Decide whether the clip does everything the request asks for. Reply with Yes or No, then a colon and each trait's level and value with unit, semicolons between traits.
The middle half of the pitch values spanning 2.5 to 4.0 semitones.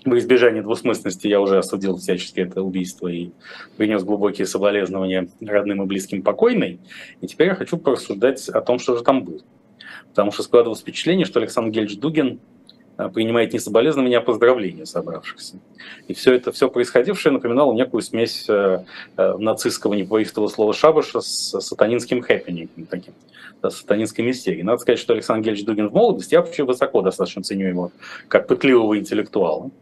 Yes: average, 3.4 semitones